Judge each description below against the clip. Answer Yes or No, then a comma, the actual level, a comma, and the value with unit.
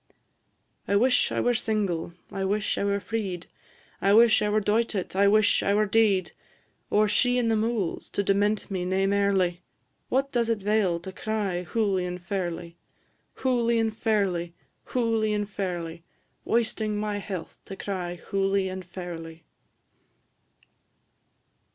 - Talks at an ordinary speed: Yes, average, 145 wpm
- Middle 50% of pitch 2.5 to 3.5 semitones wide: Yes, average, 2.9 semitones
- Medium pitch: No, high, 200 Hz